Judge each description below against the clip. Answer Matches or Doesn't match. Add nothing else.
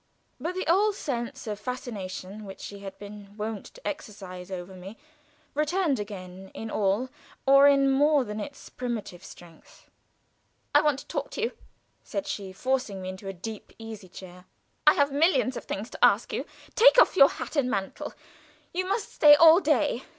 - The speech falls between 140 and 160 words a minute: Doesn't match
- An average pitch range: Doesn't match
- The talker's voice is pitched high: Matches